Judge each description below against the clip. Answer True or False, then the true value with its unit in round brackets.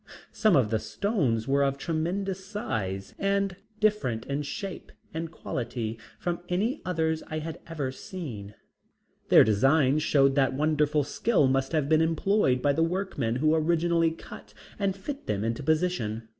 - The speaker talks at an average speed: True (155 wpm)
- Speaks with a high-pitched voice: False (155 Hz)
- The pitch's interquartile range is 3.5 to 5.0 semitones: False (5.5 semitones)